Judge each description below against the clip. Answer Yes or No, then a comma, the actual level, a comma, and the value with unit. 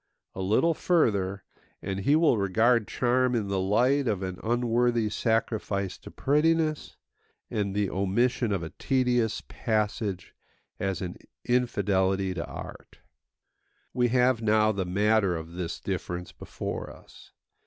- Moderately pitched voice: No, low, 105 Hz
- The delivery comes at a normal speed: No, slow, 130 wpm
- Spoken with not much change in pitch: No, average, 4.3 semitones